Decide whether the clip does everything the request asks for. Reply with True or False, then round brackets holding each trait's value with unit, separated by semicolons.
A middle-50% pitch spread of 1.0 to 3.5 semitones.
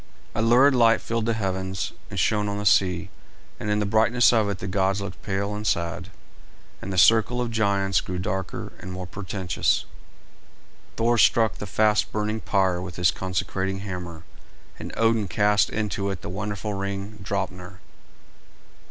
True (2.5 semitones)